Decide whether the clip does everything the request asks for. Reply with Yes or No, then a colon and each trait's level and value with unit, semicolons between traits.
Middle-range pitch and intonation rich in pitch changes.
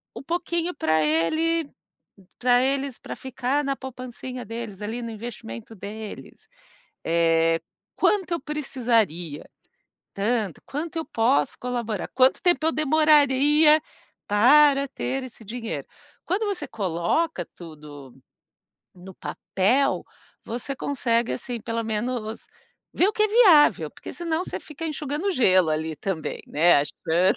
No: high, 245 Hz; wide, 7.2 semitones